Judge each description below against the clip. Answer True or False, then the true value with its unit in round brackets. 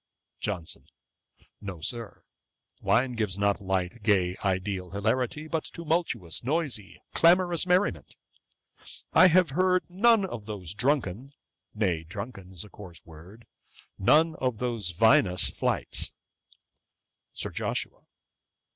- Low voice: True (110 Hz)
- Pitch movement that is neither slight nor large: False (8.4 semitones)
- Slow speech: True (110 wpm)